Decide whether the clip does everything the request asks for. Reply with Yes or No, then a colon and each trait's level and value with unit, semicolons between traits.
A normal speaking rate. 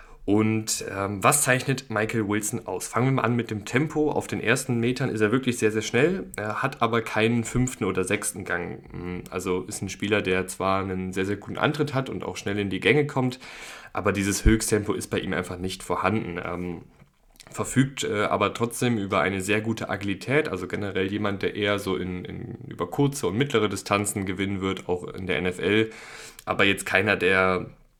No: fast, 200 wpm